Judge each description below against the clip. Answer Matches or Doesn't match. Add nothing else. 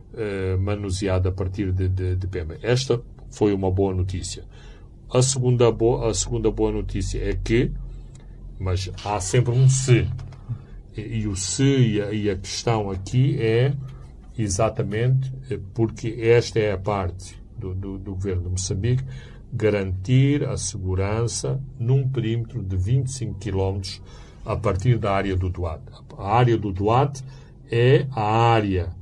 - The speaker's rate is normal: Matches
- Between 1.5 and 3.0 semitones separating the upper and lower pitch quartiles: Doesn't match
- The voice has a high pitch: Doesn't match